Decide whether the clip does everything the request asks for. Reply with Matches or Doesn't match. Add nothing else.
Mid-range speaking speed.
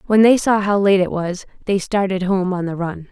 Doesn't match